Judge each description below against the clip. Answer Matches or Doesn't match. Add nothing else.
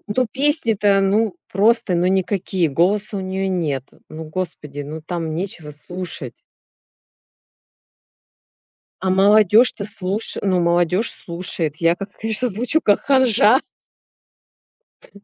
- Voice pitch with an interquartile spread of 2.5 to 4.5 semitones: Matches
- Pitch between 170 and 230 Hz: Matches